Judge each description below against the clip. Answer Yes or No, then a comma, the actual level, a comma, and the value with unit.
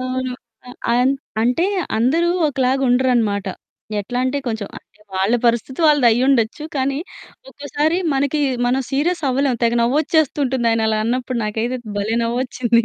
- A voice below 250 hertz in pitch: No, very high, 255 Hz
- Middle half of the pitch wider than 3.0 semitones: No, average, 2.7 semitones